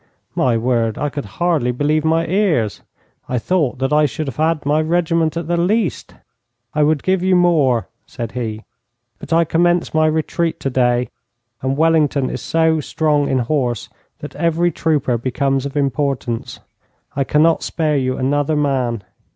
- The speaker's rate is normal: Yes, average, 160 wpm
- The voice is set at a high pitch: No, medium, 150 Hz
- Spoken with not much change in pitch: No, average, 4.1 semitones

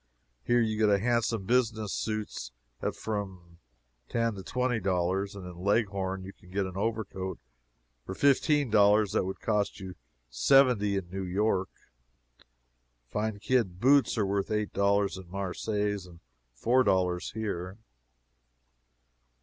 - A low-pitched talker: Yes, low, 100 Hz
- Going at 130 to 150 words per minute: Yes, slow, 135 wpm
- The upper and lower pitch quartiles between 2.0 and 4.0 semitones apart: Yes, average, 2.8 semitones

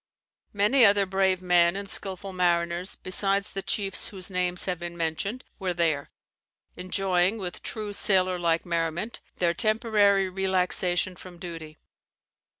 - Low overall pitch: No, medium, 185 Hz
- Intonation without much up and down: Yes, narrow, 2.2 semitones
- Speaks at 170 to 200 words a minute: No, slow, 135 wpm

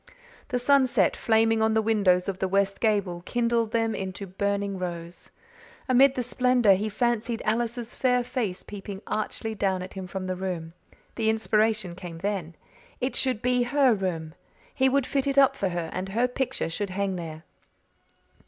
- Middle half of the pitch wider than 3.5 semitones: Yes, average, 4.4 semitones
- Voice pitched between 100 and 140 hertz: No, high, 215 Hz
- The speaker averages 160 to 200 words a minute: Yes, average, 170 wpm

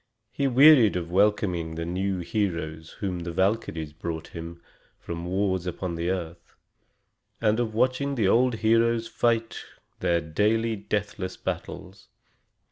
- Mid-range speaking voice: No, very low, 95 Hz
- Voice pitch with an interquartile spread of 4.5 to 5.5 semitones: Yes, average, 4.9 semitones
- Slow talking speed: Yes, slow, 130 wpm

